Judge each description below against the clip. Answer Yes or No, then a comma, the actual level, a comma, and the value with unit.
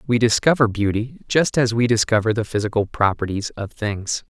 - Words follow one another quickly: No, average, 165 wpm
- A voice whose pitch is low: Yes, low, 110 Hz